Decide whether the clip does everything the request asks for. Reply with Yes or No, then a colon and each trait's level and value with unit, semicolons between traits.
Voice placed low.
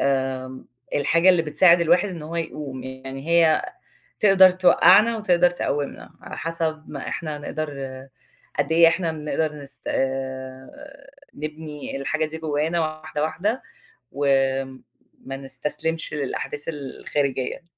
No: medium, 155 Hz